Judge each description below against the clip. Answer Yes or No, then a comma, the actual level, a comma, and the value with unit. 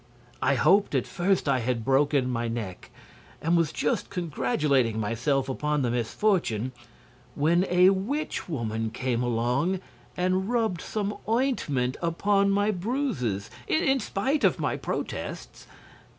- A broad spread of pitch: Yes, wide, 8.2 semitones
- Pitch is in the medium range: Yes, medium, 150 Hz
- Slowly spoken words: Yes, slow, 130 wpm